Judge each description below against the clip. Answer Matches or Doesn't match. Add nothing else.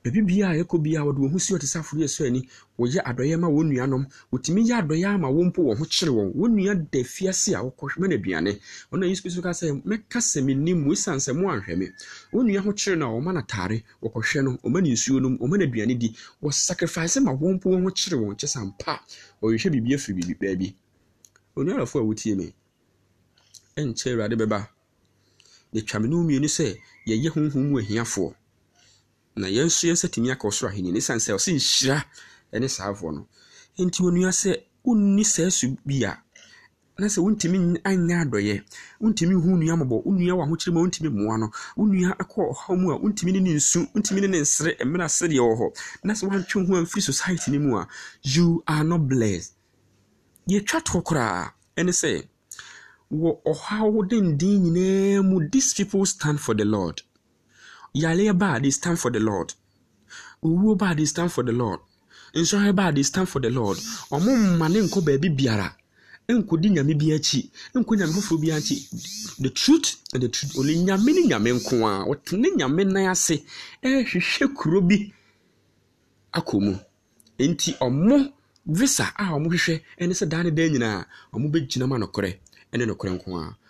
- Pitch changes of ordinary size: Doesn't match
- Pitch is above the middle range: Doesn't match